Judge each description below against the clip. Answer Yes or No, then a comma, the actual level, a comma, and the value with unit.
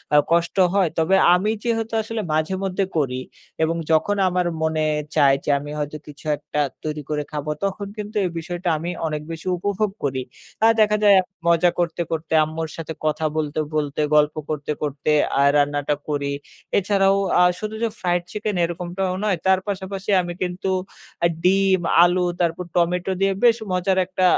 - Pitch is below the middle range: No, medium, 175 Hz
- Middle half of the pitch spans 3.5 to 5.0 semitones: Yes, average, 3.9 semitones